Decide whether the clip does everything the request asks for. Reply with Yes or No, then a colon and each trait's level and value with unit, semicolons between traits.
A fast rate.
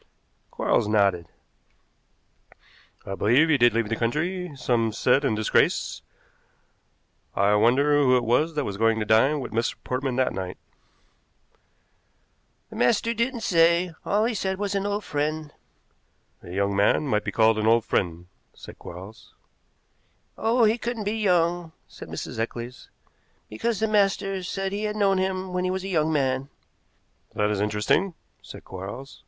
No: average, 160 wpm